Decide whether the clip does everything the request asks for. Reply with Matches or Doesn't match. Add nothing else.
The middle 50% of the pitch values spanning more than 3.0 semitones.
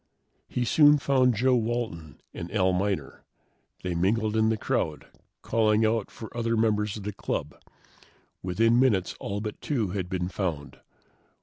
Matches